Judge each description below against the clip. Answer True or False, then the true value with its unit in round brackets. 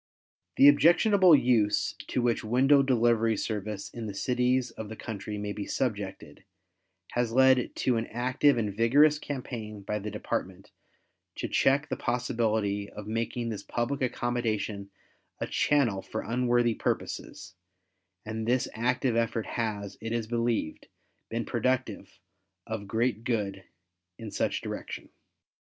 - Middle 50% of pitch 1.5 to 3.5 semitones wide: True (3.0 semitones)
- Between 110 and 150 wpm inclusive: True (135 wpm)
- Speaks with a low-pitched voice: True (115 Hz)